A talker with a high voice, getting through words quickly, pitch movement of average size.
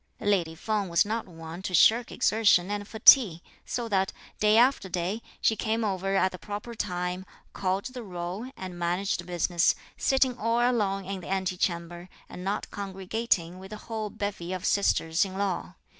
No: high, 195 Hz; average, 175 wpm; average, 3.3 semitones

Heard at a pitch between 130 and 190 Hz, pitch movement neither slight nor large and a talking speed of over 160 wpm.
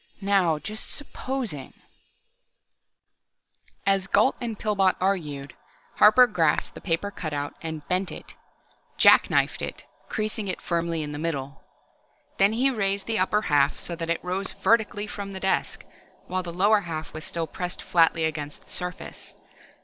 No: medium, 185 Hz; average, 4.3 semitones; average, 155 wpm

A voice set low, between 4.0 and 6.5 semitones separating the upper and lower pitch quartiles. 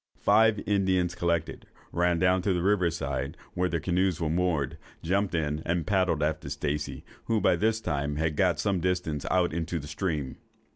No: very low, 85 Hz; average, 3.3 semitones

